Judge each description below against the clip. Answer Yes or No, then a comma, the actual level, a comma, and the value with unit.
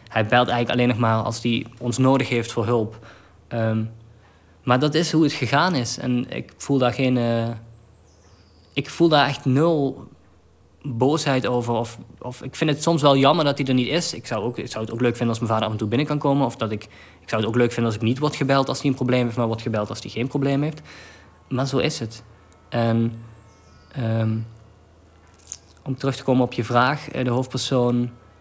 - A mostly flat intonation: No, average, 3.2 semitones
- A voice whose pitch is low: Yes, low, 120 Hz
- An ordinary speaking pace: No, fast, 230 wpm